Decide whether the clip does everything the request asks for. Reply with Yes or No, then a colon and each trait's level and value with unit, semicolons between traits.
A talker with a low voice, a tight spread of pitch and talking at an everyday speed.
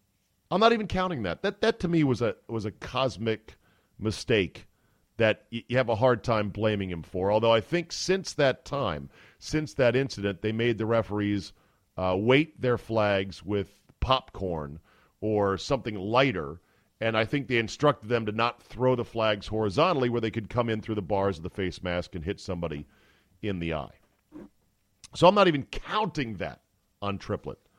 No: low, 110 Hz; average, 4.6 semitones; average, 180 wpm